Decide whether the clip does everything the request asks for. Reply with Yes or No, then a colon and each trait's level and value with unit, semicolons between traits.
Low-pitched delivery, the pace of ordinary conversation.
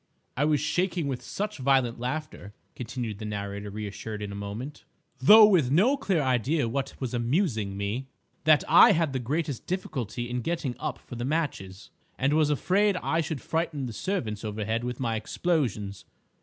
Yes: low, 130 Hz; average, 170 wpm